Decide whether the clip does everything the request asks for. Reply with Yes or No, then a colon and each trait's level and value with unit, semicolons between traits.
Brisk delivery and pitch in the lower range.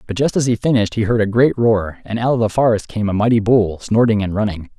Yes: fast, 275 wpm; low, 110 Hz